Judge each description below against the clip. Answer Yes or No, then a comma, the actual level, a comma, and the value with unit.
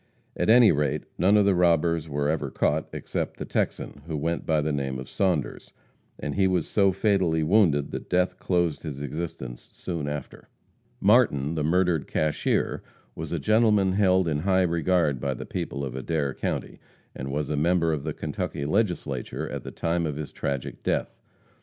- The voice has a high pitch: No, very low, 80 Hz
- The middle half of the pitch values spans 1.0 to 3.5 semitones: No, average, 4.1 semitones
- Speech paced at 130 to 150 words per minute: No, average, 180 wpm